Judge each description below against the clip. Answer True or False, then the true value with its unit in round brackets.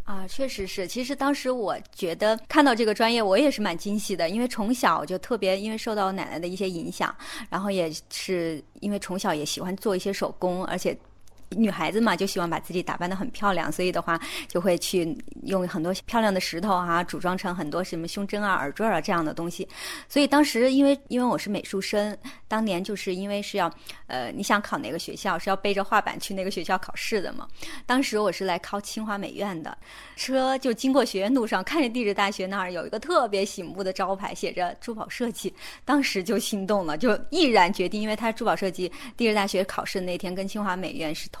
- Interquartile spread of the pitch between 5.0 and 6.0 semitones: False (3.8 semitones)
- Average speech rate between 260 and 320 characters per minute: False (335 characters per minute)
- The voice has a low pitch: False (200 Hz)